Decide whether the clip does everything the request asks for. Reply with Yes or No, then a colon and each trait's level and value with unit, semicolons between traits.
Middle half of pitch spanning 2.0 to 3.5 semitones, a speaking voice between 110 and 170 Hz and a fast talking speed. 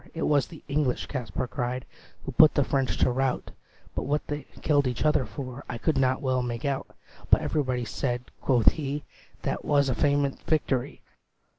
No: narrow, 2.5 semitones; low, 135 Hz; average, 185 wpm